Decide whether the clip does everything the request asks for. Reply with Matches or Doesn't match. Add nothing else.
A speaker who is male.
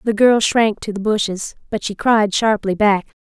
Doesn't match